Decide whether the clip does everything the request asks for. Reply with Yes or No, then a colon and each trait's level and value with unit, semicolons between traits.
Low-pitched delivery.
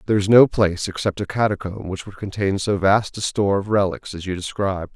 Yes: low, 100 Hz